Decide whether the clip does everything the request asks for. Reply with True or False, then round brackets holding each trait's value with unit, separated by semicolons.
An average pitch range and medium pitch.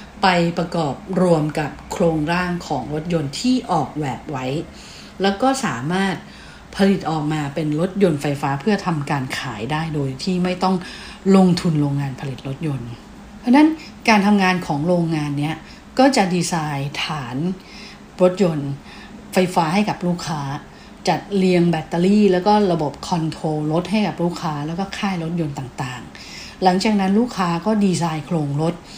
True (4.2 semitones; 170 Hz)